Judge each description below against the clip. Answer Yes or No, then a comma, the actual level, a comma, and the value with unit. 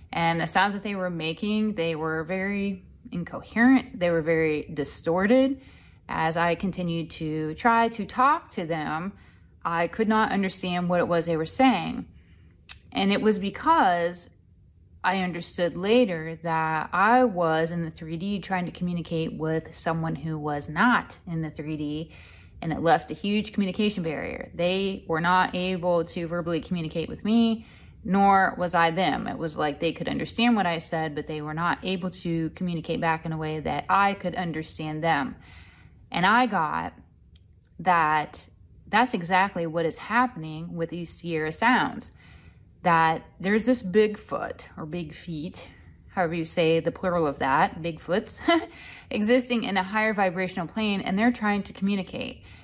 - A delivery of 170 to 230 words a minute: No, average, 160 wpm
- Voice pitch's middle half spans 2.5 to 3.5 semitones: No, average, 4.0 semitones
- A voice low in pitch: No, medium, 170 Hz